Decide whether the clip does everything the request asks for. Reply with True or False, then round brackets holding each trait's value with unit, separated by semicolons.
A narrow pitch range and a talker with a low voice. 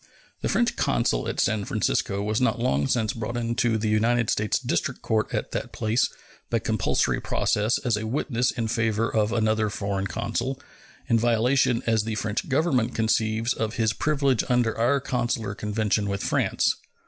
True (2.0 semitones; 110 Hz)